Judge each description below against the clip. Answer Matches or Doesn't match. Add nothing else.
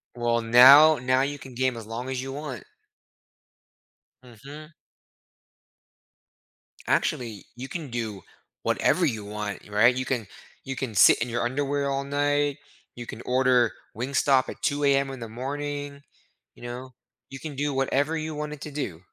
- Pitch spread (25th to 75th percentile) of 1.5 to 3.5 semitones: Matches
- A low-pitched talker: Matches